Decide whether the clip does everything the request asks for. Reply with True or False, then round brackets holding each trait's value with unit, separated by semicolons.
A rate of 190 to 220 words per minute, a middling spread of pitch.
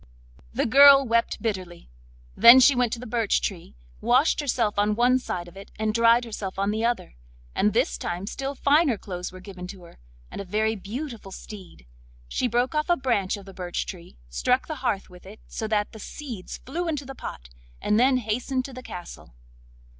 True (200 wpm; 4.8 semitones)